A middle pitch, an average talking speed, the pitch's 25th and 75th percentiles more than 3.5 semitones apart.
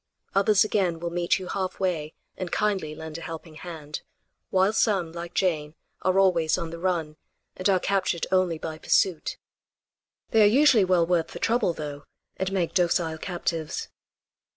No: medium, 175 Hz; average, 165 wpm; average, 2.8 semitones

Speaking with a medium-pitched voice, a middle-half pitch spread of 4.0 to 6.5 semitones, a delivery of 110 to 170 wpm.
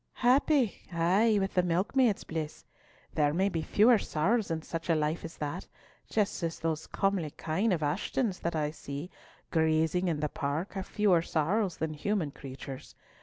Yes: medium, 170 Hz; average, 4.3 semitones; average, 160 wpm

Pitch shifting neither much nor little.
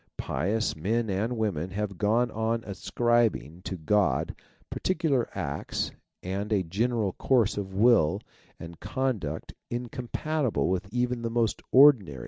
Yes: average, 4.1 semitones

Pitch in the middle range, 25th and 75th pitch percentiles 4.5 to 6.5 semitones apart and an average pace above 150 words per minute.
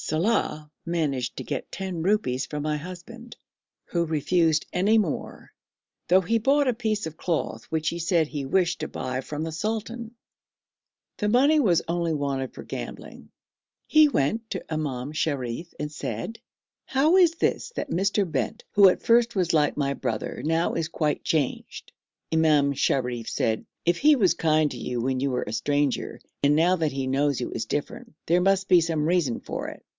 Yes: medium, 165 Hz; wide, 5.4 semitones; average, 180 wpm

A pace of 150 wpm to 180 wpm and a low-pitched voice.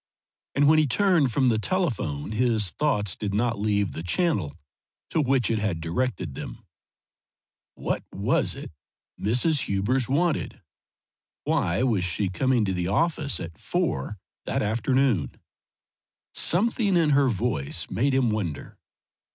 No: slow, 135 wpm; low, 115 Hz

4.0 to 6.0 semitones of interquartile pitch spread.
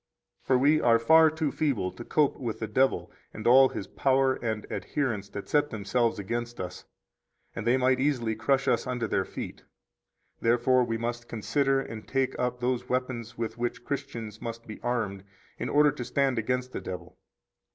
No: average, 2.8 semitones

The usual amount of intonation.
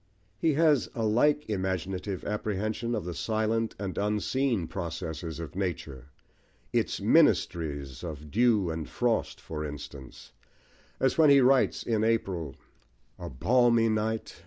No: wide, 5.9 semitones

